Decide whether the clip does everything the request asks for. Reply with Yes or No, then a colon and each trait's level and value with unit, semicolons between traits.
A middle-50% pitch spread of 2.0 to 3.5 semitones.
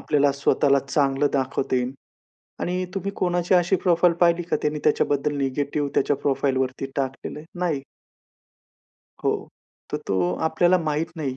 No: average, 4.0 semitones